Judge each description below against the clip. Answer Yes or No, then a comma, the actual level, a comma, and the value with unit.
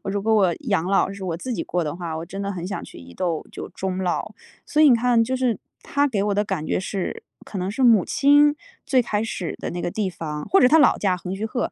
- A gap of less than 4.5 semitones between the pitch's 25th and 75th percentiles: No, average, 5.1 semitones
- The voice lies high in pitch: Yes, high, 200 Hz